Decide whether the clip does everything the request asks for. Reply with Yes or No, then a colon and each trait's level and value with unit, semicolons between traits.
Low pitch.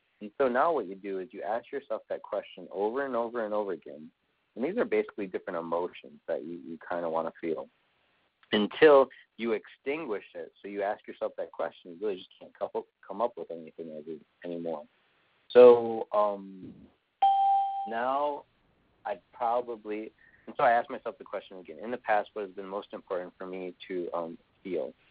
Yes: low, 120 Hz